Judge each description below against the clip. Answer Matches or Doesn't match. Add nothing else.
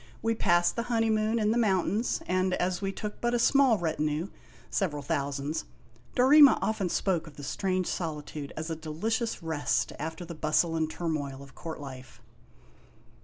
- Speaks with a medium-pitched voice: Matches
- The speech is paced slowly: Doesn't match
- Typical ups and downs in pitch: Doesn't match